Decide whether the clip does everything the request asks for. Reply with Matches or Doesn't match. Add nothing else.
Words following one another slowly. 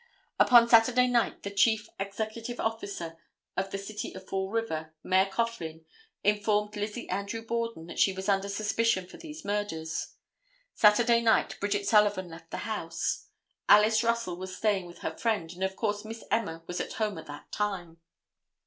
Doesn't match